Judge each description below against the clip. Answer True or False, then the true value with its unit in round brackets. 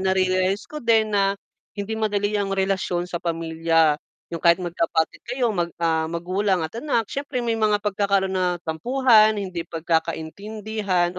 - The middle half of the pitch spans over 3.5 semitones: True (4.0 semitones)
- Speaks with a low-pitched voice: False (190 Hz)